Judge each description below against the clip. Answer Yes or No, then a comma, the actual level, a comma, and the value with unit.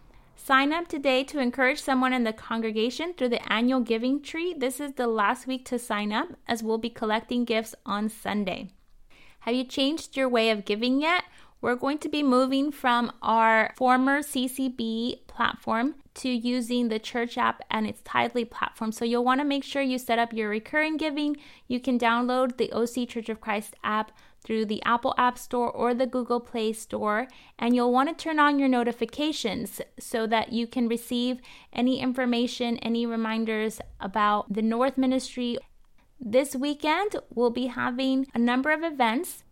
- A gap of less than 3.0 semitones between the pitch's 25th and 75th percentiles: Yes, narrow, 2.6 semitones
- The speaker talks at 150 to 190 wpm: Yes, average, 180 wpm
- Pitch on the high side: Yes, high, 245 Hz